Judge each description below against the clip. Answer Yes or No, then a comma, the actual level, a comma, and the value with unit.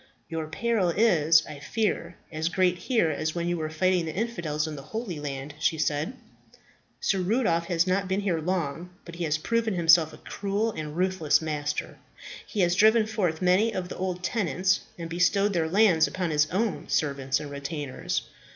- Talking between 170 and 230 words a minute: Yes, average, 185 wpm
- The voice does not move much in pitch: No, average, 3.6 semitones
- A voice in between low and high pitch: Yes, medium, 175 Hz